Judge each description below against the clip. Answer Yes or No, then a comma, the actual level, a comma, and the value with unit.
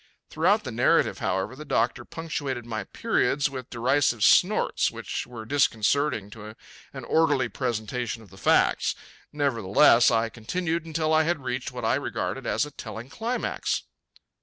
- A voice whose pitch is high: No, low, 125 Hz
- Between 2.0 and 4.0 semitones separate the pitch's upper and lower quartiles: No, average, 4.6 semitones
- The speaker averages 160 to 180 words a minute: No, average, 150 wpm